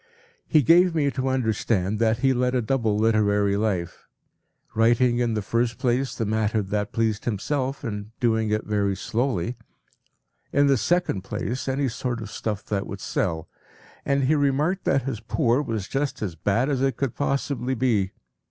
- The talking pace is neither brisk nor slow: Yes, average, 170 wpm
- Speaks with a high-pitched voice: No, low, 115 Hz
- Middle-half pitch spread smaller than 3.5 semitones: No, average, 4.2 semitones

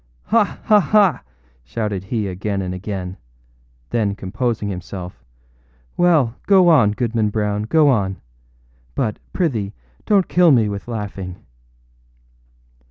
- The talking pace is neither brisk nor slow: No, slow, 115 wpm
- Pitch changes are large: Yes, wide, 6.8 semitones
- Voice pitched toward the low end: Yes, low, 105 Hz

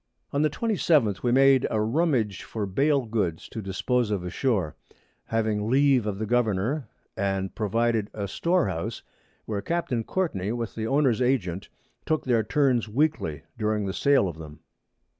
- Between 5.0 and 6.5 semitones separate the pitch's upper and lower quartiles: Yes, average, 5.3 semitones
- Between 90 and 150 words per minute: No, average, 160 wpm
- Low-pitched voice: Yes, low, 115 Hz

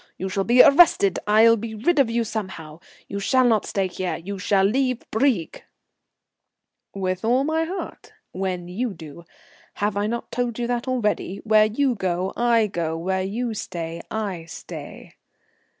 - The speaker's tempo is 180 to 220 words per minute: No, average, 165 wpm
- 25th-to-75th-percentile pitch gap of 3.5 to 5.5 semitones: Yes, average, 4.2 semitones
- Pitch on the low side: No, high, 210 Hz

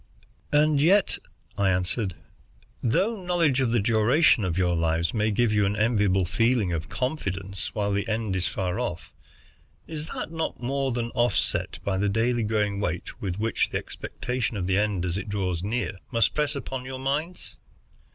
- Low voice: Yes, low, 110 Hz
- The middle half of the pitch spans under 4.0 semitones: No, average, 5.2 semitones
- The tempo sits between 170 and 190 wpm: Yes, average, 175 wpm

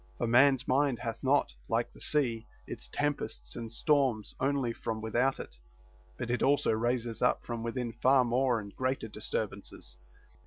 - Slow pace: No, average, 160 wpm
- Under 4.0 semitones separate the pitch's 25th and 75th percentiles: Yes, average, 2.9 semitones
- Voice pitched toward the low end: Yes, low, 120 Hz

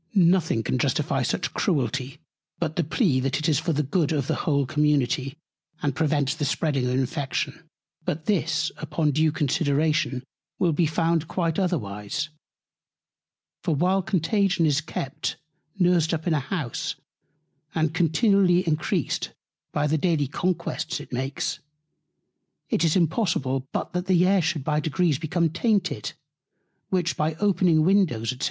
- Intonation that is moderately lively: Yes, average, 3.6 semitones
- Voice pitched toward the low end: No, medium, 155 Hz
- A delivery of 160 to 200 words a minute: No, average, 145 wpm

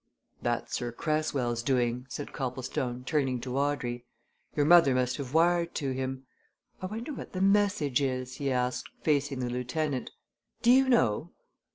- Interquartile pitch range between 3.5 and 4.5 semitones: Yes, average, 3.9 semitones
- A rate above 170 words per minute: No, average, 155 wpm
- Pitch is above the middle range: No, low, 135 Hz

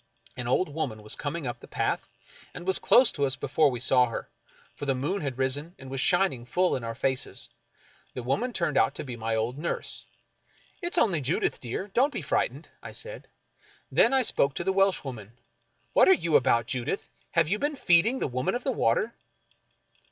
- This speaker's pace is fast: Yes, fast, 210 wpm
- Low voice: No, medium, 145 Hz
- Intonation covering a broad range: Yes, wide, 7.1 semitones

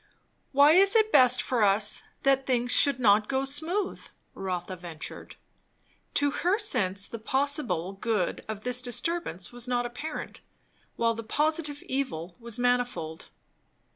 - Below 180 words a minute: Yes, average, 140 wpm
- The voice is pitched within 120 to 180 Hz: No, high, 245 Hz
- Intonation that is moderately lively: No, wide, 5.7 semitones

